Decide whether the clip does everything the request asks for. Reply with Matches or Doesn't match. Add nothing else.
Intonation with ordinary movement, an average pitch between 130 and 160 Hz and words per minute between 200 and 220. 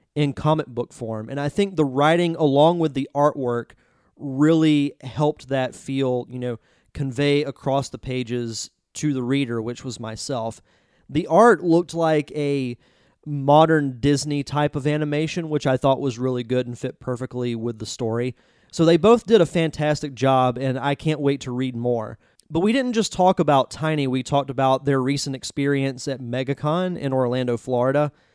Doesn't match